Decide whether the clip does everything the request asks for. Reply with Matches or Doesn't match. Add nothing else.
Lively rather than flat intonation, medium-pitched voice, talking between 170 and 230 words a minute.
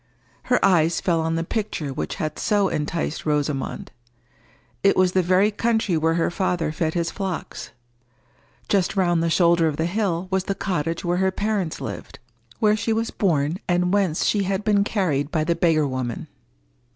Doesn't match